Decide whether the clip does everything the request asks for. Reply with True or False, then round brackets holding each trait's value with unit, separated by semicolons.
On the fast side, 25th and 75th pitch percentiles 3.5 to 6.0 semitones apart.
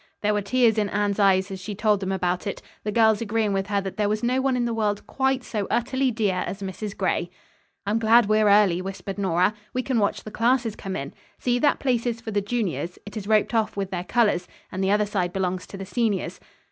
False (240 wpm; 2.9 semitones)